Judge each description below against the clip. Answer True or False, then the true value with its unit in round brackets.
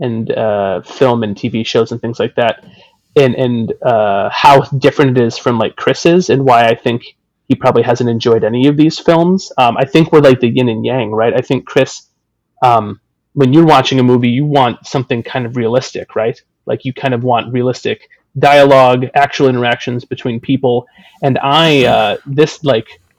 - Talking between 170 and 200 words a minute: True (195 wpm)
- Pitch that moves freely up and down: False (2.8 semitones)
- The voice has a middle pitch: False (125 Hz)